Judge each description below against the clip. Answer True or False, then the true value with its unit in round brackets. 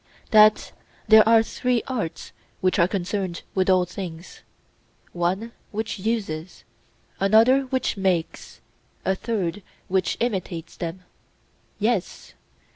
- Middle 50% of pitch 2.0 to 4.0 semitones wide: True (3.7 semitones)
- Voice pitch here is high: True (195 Hz)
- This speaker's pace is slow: True (110 wpm)